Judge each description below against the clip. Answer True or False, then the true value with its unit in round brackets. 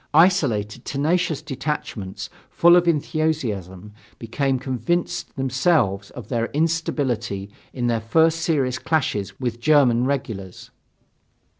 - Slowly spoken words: True (105 wpm)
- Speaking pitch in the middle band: False (130 Hz)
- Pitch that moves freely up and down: True (5.7 semitones)